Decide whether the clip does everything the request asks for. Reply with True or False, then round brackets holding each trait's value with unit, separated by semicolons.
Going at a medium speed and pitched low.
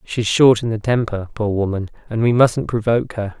False (210 wpm; 110 Hz)